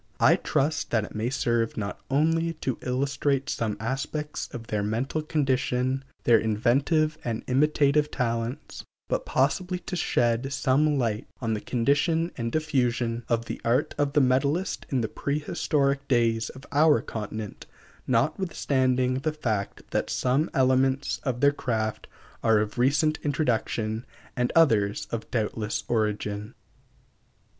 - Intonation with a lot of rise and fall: No, average, 4.1 semitones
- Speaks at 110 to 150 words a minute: Yes, slow, 135 wpm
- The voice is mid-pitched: No, low, 130 Hz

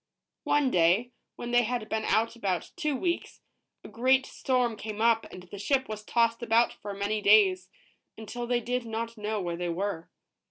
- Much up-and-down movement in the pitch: No, average, 3.2 semitones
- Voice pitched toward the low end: No, high, 225 Hz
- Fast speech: No, average, 185 wpm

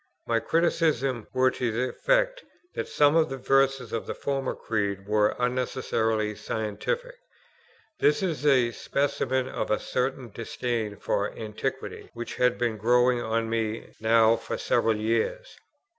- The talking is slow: No, average, 145 wpm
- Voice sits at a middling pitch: No, low, 125 Hz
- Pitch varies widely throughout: No, average, 3.5 semitones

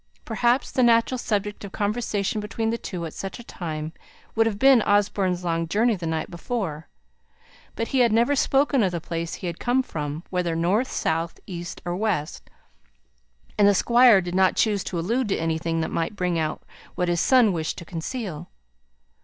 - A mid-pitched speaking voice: No, high, 195 Hz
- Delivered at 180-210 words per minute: Yes, average, 185 wpm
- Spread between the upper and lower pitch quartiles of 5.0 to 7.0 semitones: Yes, wide, 5.4 semitones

